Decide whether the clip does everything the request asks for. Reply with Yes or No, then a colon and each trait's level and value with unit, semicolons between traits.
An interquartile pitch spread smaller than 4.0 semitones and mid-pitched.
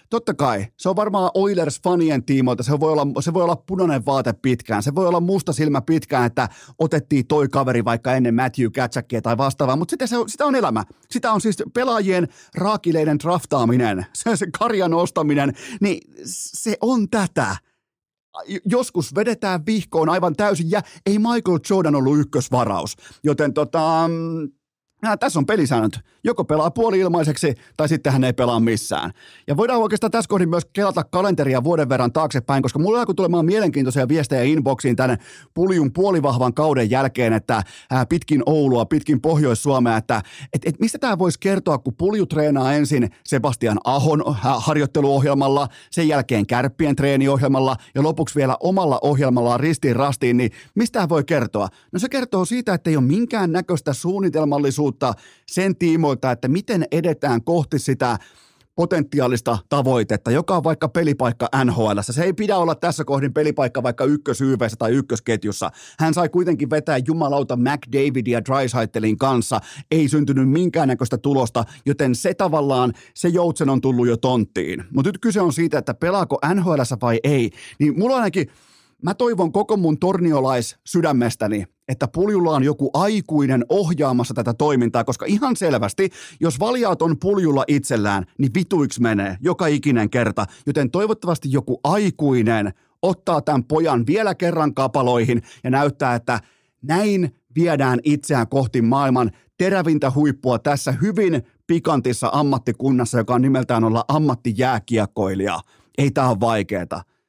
No: wide, 5.4 semitones; medium, 145 Hz